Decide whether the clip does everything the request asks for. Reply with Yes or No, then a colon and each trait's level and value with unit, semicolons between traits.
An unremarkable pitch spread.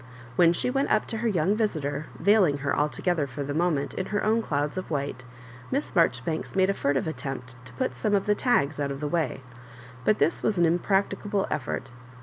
No: wide, 6.0 semitones